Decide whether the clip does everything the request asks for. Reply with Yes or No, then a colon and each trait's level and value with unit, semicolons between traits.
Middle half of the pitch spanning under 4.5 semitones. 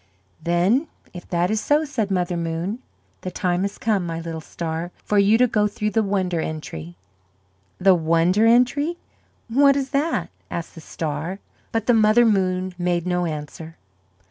No: average, 4.8 semitones